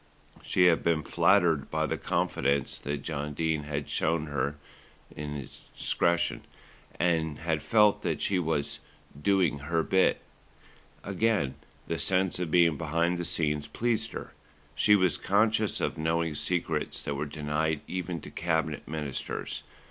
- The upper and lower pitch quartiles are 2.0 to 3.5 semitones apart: Yes, average, 3.2 semitones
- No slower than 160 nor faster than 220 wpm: No, average, 140 wpm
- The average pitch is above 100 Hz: No, very low, 80 Hz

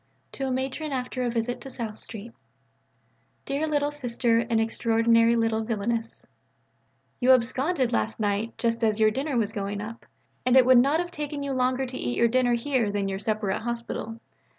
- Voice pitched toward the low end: No, high, 235 Hz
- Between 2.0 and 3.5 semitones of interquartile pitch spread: Yes, average, 2.7 semitones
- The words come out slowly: No, average, 185 wpm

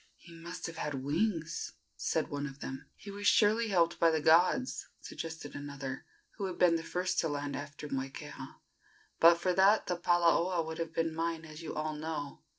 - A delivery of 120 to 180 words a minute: No, average, 190 wpm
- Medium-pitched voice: Yes, medium, 165 Hz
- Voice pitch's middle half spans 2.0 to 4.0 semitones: Yes, average, 3.2 semitones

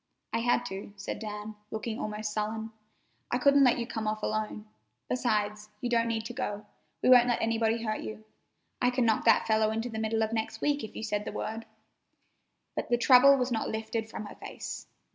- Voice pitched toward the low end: No, high, 225 Hz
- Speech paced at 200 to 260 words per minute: Yes, fast, 205 wpm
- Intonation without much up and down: Yes, narrow, 1.9 semitones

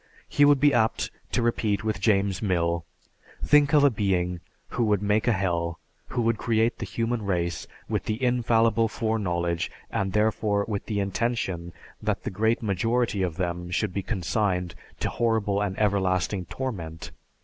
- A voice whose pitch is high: No, low, 105 Hz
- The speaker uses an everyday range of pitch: Yes, average, 3.9 semitones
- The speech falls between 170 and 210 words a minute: No, average, 160 wpm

